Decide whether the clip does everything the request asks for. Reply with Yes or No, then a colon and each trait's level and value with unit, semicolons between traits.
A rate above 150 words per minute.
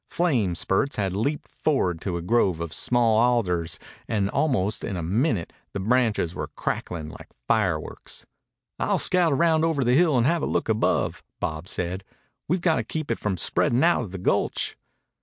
Yes: average, 180 wpm